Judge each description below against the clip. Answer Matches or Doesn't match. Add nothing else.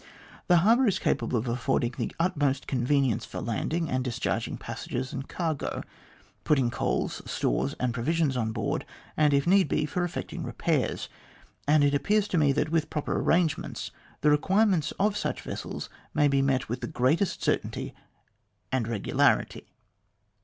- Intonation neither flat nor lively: Matches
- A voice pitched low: Doesn't match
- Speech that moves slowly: Doesn't match